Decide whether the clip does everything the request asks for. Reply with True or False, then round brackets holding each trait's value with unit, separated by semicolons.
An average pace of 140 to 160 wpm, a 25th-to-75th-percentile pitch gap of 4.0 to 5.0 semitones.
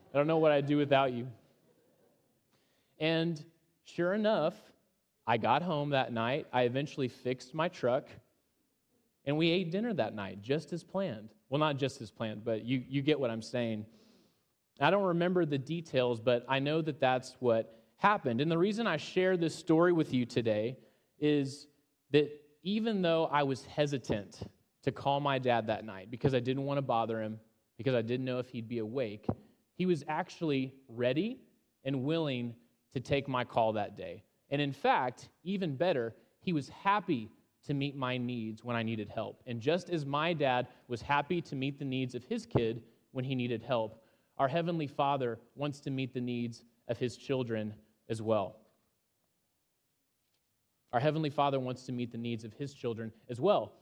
False (185 wpm; 4.5 semitones)